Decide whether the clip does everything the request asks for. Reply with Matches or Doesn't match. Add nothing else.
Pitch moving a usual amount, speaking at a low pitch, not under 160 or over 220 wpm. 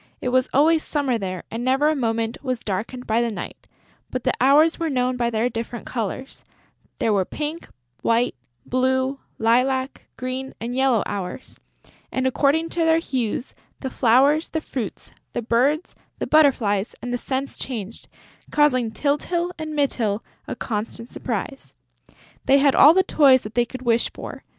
Doesn't match